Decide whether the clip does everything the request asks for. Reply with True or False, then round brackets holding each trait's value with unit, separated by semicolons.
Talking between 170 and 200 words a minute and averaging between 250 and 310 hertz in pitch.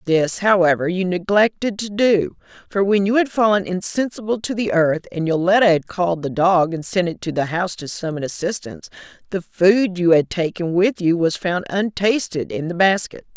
False (195 wpm; 185 Hz)